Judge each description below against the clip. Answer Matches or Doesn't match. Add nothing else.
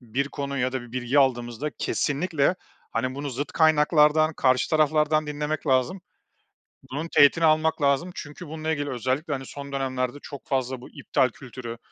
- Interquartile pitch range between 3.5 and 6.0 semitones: Doesn't match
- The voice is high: Doesn't match